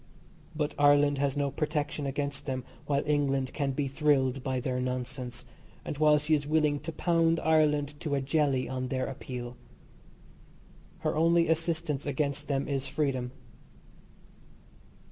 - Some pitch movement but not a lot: No, narrow, 2.2 semitones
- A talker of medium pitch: Yes, medium, 145 Hz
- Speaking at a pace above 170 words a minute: No, average, 145 wpm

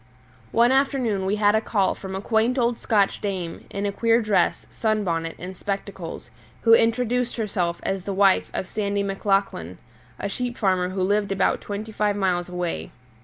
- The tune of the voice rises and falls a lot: No, average, 2.8 semitones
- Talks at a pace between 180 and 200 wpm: No, average, 170 wpm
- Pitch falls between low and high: No, high, 200 Hz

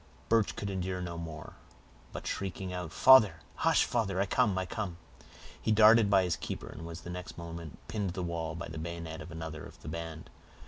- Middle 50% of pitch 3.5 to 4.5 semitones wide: No, average, 3.1 semitones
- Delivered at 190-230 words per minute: Yes, average, 195 wpm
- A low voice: Yes, very low, 90 Hz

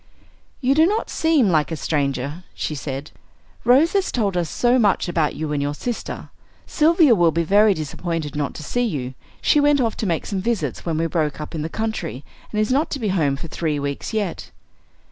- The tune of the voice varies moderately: No, wide, 7.9 semitones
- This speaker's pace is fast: Yes, fast, 210 wpm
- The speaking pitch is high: No, medium, 175 Hz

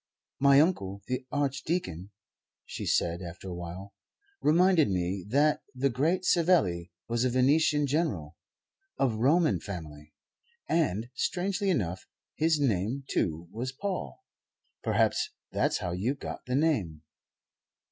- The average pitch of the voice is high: No, low, 125 Hz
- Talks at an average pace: No, slow, 125 wpm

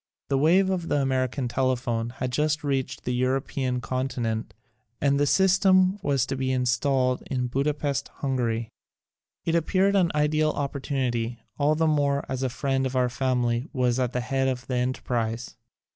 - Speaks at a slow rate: No, average, 170 wpm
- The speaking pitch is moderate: No, low, 130 Hz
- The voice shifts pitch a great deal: No, narrow, 2.6 semitones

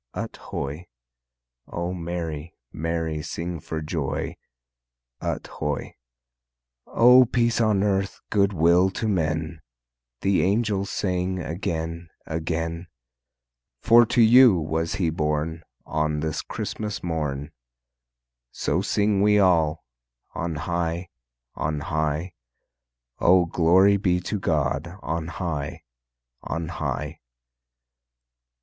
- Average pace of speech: No, slow, 105 wpm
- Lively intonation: No, average, 3.5 semitones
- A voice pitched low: Yes, very low, 85 Hz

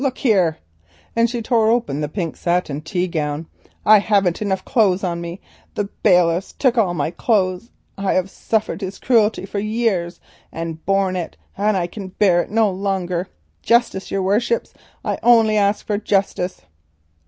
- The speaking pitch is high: Yes, high, 195 Hz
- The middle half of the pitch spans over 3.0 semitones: Yes, average, 3.4 semitones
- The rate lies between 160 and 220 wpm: Yes, average, 165 wpm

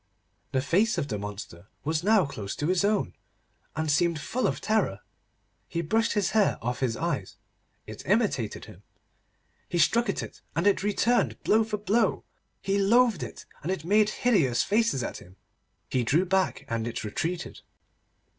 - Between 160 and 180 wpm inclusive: Yes, average, 170 wpm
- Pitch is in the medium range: Yes, medium, 175 Hz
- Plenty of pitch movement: Yes, wide, 8.2 semitones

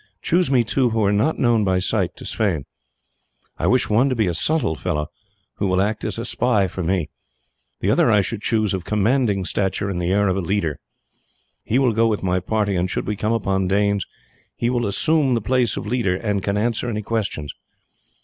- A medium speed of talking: No, fast, 215 wpm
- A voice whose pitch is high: No, low, 105 Hz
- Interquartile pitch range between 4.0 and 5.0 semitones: No, average, 3.5 semitones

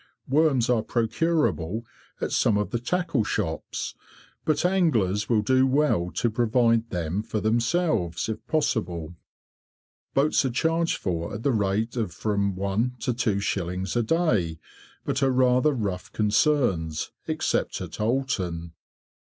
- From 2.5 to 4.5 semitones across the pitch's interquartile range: No, average, 5.3 semitones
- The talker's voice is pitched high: No, low, 115 Hz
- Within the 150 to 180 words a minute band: No, slow, 135 wpm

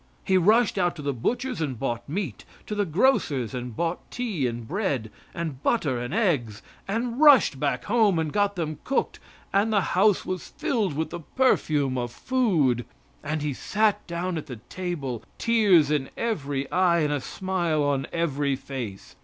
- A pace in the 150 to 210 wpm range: Yes, average, 175 wpm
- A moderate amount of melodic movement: No, wide, 6.9 semitones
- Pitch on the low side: No, medium, 165 Hz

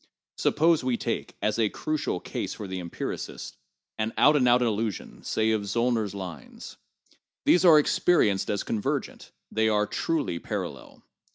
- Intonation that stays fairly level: No, average, 4.2 semitones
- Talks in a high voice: No, low, 110 Hz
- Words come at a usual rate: Yes, average, 155 wpm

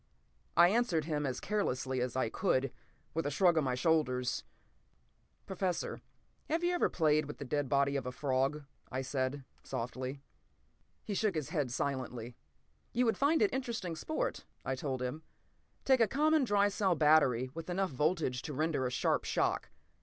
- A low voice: No, medium, 150 Hz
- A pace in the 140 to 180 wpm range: Yes, average, 170 wpm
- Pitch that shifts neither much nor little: No, wide, 6.7 semitones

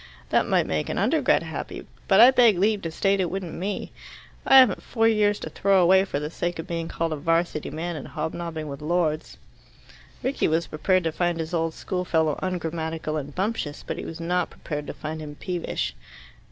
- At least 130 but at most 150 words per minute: No, average, 200 wpm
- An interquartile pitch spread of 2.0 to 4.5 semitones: Yes, average, 3.1 semitones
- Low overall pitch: No, medium, 170 Hz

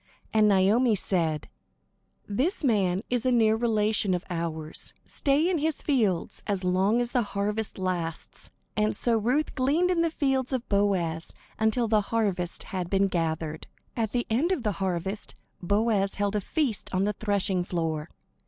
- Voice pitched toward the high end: Yes, high, 210 Hz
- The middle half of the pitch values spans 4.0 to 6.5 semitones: Yes, average, 4.5 semitones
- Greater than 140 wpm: Yes, average, 160 wpm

